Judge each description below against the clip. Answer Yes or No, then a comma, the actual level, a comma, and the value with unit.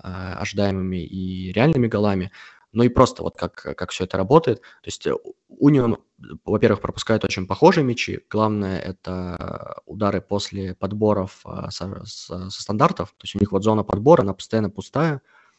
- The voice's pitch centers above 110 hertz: No, low, 100 Hz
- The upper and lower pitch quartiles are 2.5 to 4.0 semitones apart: Yes, average, 3.2 semitones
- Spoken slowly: No, average, 155 wpm